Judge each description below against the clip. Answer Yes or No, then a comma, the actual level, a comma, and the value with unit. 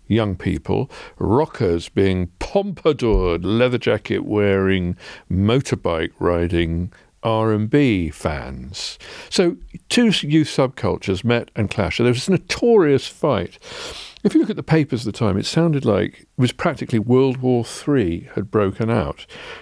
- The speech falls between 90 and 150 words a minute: Yes, average, 145 wpm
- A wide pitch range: Yes, wide, 6.0 semitones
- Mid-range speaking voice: No, low, 110 Hz